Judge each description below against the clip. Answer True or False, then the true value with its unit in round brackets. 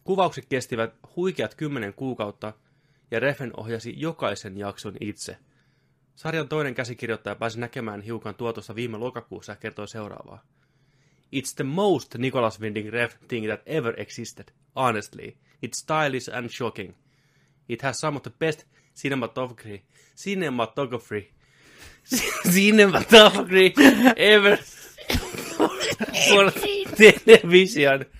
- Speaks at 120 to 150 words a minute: False (105 wpm)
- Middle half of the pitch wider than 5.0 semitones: True (5.5 semitones)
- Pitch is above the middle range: False (135 Hz)